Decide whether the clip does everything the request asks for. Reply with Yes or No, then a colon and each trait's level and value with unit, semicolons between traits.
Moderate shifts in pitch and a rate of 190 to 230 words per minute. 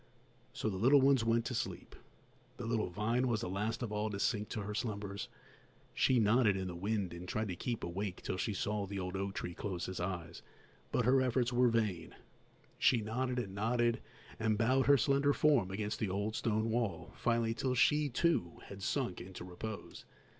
Yes: average, 3.9 semitones; average, 195 wpm